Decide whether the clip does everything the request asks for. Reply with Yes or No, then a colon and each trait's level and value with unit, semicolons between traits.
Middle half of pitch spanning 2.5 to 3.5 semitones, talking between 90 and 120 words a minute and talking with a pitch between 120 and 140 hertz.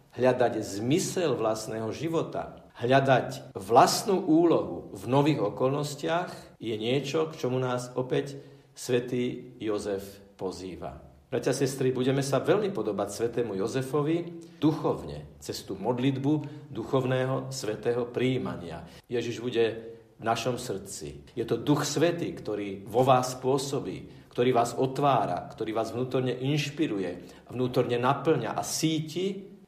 No: average, 4.3 semitones; average, 115 wpm; low, 130 Hz